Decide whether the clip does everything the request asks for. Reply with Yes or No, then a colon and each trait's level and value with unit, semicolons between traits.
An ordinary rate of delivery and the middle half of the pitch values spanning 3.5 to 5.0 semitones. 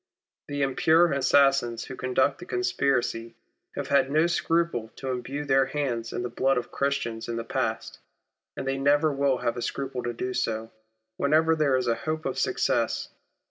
No: average, 175 wpm; average, 2.7 semitones